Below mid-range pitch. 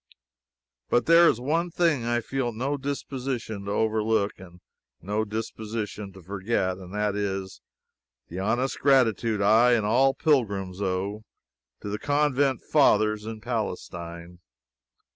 Yes: low, 110 Hz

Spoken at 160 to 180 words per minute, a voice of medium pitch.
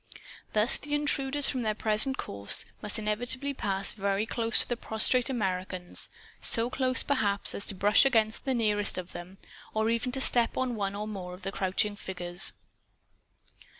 No: average, 170 wpm; high, 215 Hz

